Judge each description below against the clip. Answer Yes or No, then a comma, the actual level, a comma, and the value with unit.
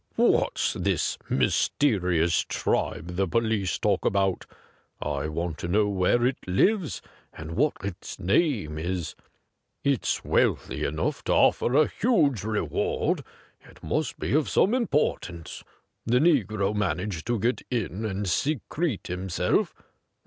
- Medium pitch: No, low, 100 Hz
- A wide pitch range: Yes, wide, 6.7 semitones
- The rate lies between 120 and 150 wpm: Yes, slow, 135 wpm